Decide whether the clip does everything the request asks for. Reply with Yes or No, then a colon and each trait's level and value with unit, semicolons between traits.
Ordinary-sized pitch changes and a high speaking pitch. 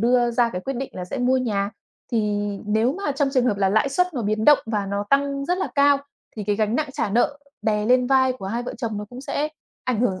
Yes: average, 4.5 semitones; high, 245 Hz